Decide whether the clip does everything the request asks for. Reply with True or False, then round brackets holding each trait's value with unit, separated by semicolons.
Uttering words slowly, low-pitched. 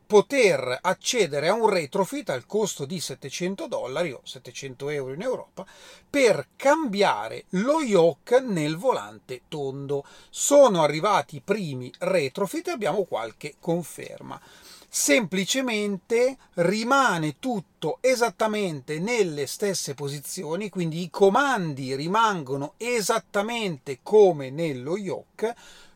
False (105 wpm; 190 Hz)